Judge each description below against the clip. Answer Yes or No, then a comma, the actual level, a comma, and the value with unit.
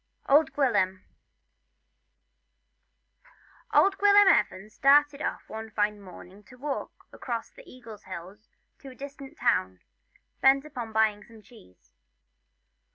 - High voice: Yes, high, 235 Hz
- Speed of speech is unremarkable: No, slow, 115 wpm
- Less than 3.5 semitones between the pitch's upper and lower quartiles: No, average, 5.3 semitones